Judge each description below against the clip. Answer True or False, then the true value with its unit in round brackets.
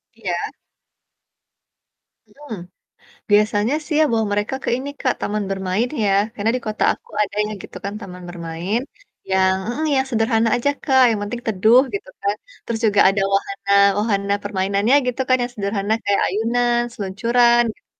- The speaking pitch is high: True (215 Hz)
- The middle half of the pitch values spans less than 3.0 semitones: False (3.3 semitones)